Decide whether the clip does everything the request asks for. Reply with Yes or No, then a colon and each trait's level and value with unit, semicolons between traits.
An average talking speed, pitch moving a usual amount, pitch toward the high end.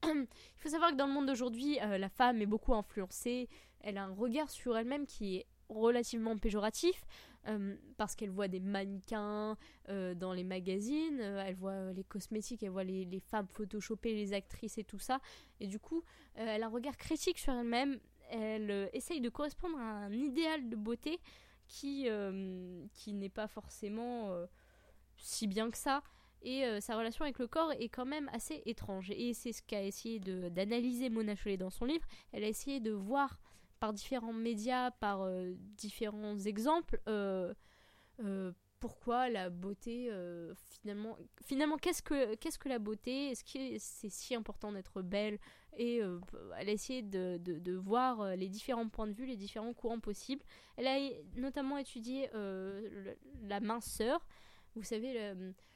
Yes: average, 180 wpm; average, 4.1 semitones; high, 220 Hz